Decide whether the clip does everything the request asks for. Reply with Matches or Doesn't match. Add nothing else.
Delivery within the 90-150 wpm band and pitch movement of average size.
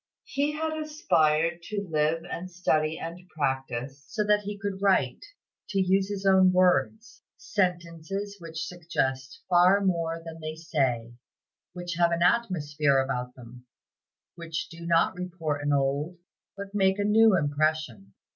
Matches